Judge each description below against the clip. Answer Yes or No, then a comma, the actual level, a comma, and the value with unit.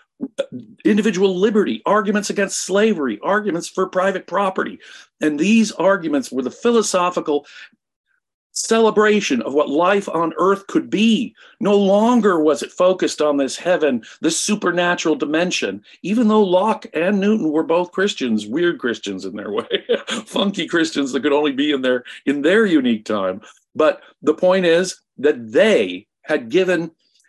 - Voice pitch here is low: No, medium, 185 Hz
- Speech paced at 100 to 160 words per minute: Yes, average, 145 wpm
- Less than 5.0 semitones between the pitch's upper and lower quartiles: No, wide, 5.6 semitones